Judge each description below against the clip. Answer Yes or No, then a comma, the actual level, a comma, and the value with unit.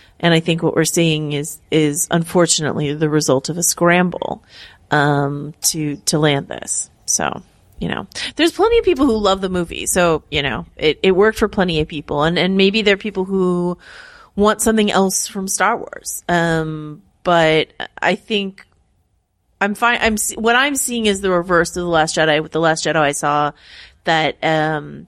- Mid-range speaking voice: Yes, medium, 170 Hz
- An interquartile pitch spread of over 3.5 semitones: Yes, average, 4.3 semitones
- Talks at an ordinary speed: Yes, average, 185 wpm